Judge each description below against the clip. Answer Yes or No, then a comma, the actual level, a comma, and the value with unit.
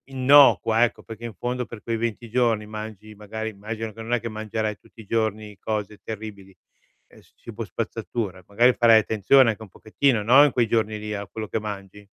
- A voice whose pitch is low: Yes, low, 110 Hz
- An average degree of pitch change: No, narrow, 1.7 semitones